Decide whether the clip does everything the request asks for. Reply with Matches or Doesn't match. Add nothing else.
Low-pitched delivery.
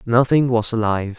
Matches